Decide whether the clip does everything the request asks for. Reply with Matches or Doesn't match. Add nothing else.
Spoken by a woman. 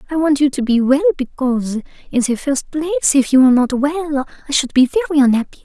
Matches